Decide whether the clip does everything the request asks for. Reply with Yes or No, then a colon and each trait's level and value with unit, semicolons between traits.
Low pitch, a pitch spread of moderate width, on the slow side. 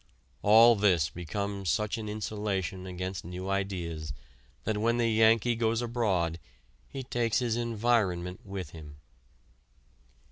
Yes: low, 100 Hz; average, 4.0 semitones; slow, 120 wpm